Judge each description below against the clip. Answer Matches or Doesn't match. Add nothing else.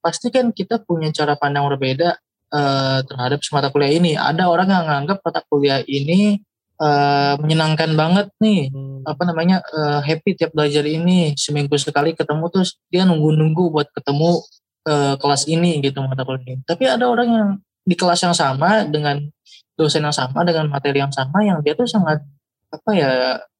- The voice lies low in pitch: Doesn't match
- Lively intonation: Doesn't match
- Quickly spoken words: Matches